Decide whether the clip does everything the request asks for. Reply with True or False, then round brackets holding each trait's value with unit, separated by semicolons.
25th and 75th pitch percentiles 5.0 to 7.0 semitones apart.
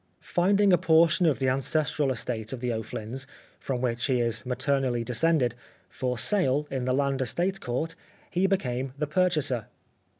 False (4.5 semitones)